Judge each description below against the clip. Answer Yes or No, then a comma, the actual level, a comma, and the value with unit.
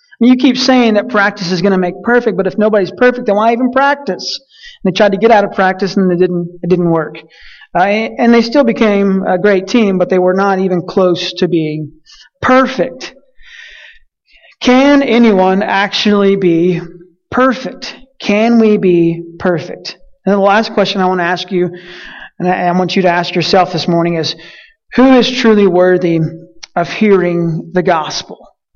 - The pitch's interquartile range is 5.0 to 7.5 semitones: No, average, 4.6 semitones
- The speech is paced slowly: No, average, 180 wpm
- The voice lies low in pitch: No, high, 195 Hz